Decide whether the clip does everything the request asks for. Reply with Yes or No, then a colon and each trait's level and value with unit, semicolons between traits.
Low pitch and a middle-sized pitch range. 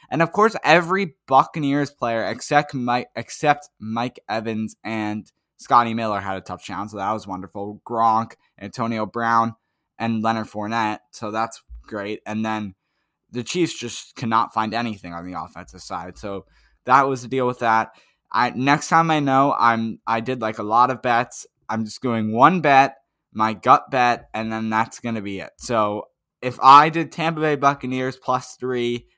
Yes: low, 115 Hz; average, 3.6 semitones